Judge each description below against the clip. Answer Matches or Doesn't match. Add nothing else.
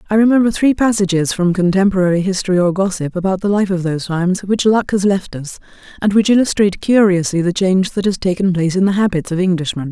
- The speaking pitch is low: Doesn't match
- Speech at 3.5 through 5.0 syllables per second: Doesn't match